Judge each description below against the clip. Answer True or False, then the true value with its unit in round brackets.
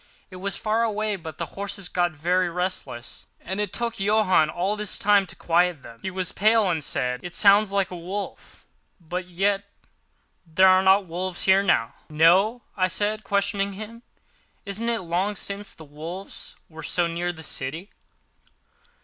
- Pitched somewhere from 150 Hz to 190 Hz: True (185 Hz)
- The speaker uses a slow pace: False (165 wpm)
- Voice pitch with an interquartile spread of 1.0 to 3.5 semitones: True (2.9 semitones)